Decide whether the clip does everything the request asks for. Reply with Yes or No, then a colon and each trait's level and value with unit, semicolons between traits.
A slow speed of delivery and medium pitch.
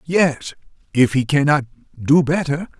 Yes: slow, 130 wpm; medium, 145 Hz